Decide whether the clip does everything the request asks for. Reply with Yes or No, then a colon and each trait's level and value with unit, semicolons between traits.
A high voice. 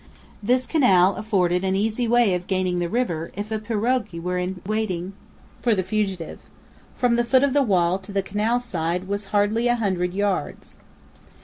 Yes: high, 205 Hz